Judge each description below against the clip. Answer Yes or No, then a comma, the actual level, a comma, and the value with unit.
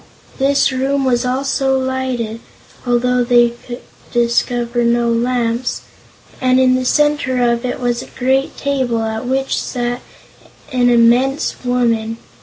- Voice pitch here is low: No, high, 245 Hz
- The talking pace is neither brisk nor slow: No, slow, 130 wpm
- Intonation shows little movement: Yes, narrow, 1.7 semitones